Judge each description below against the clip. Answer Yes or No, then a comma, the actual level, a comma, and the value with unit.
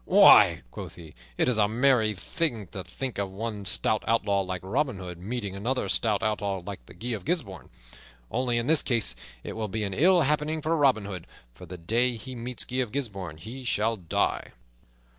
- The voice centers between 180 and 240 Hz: No, low, 110 Hz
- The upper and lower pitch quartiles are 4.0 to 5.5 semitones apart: Yes, average, 4.6 semitones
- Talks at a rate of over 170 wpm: Yes, average, 195 wpm